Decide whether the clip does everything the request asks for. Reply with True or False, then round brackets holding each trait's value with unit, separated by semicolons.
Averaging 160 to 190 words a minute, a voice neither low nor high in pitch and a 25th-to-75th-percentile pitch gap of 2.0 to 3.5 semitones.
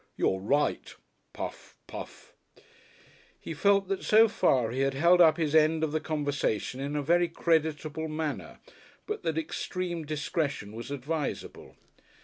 False (140 wpm; 155 Hz; 2.7 semitones)